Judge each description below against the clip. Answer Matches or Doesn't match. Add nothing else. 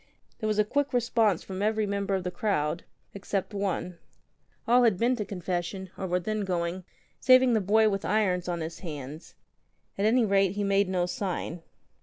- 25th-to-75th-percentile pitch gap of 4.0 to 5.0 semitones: Doesn't match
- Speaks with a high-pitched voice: Matches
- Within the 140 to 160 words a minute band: Doesn't match